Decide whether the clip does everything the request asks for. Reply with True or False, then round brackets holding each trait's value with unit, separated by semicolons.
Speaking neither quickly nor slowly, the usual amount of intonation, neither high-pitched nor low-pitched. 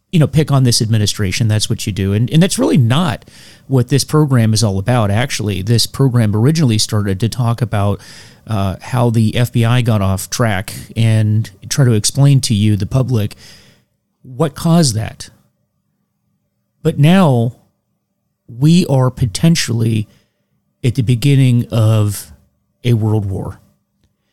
False (145 wpm; 3.7 semitones; 115 Hz)